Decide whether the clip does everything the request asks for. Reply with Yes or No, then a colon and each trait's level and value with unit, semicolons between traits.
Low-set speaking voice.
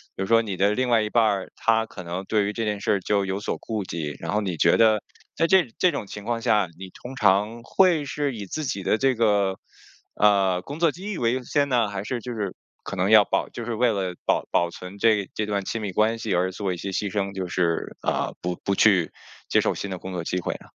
Yes: low, 105 Hz